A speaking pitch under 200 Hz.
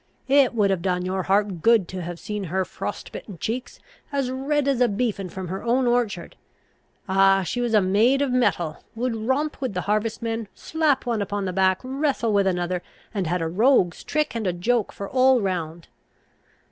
No: high, 210 Hz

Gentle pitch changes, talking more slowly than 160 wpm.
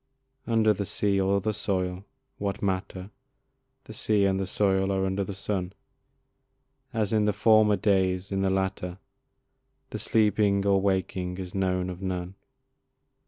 Yes: narrow, 1.5 semitones; average, 150 wpm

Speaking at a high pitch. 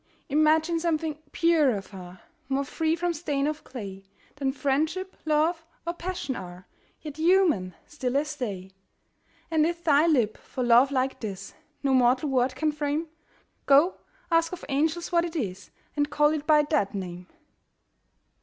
Yes: very high, 295 Hz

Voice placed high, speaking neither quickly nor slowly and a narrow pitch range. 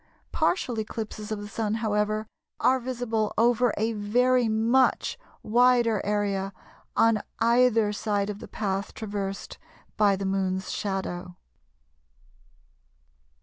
No: high, 215 Hz; slow, 110 wpm; narrow, 2.2 semitones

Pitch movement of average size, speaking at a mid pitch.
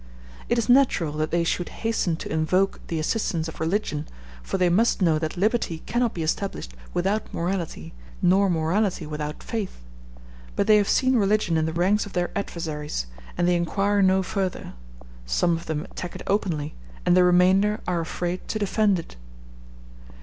Yes: average, 4.0 semitones; medium, 180 Hz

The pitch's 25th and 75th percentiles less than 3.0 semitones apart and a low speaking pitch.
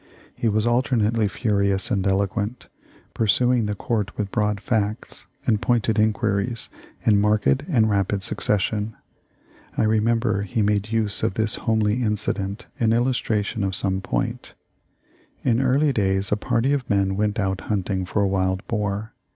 Yes: narrow, 2.4 semitones; low, 105 Hz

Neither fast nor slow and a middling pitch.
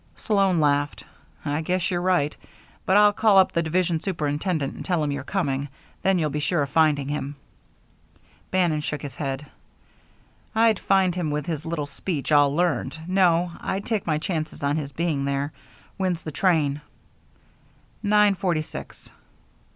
Yes: average, 160 wpm; medium, 160 Hz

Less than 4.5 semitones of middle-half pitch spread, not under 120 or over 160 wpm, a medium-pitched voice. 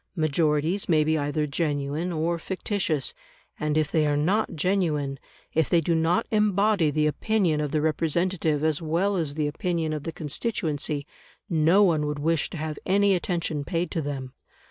No: average, 3.0 semitones; average, 170 wpm; medium, 160 Hz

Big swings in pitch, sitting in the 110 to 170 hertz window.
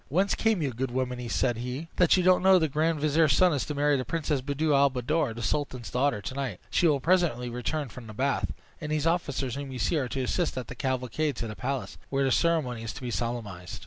No: average, 4.0 semitones; low, 135 Hz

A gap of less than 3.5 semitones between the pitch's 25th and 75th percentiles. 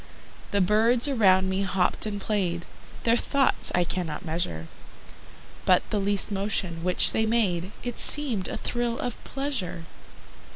No: average, 4.4 semitones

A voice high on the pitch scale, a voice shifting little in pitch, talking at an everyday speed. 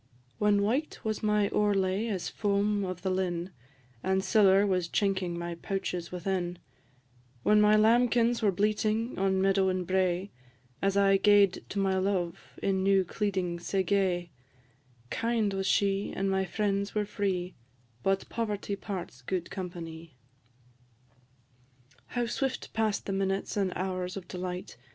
Yes: high, 195 Hz; narrow, 2.0 semitones; average, 145 wpm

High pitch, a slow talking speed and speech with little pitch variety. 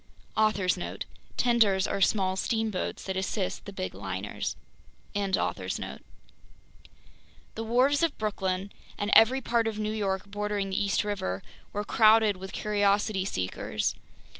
Yes: high, 205 Hz; slow, 130 wpm; narrow, 2.3 semitones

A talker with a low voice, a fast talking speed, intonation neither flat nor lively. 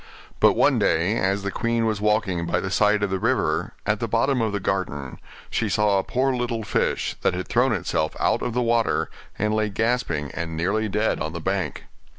Yes: low, 105 Hz; fast, 210 wpm; average, 3.4 semitones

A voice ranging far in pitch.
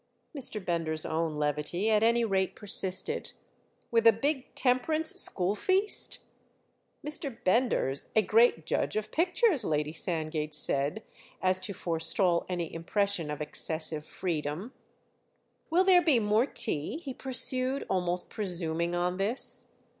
Yes: wide, 7.0 semitones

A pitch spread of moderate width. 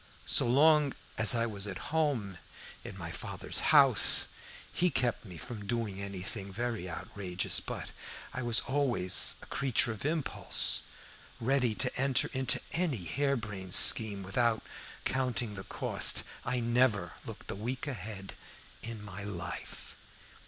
Yes: average, 4.7 semitones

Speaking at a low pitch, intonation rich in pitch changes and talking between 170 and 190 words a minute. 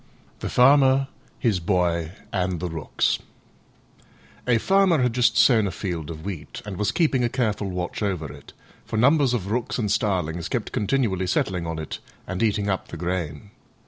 Yes: low, 100 Hz; wide, 5.7 semitones; average, 175 wpm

